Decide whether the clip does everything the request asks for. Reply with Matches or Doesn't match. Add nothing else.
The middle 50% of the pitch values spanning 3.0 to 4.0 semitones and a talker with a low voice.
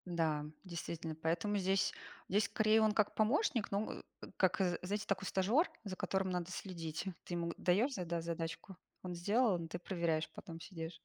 Doesn't match